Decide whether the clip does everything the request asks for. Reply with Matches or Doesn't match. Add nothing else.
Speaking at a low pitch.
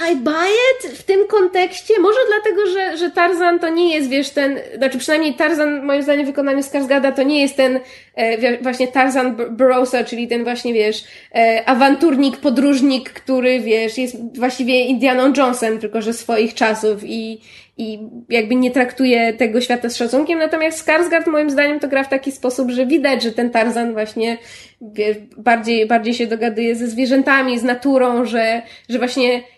Doesn't match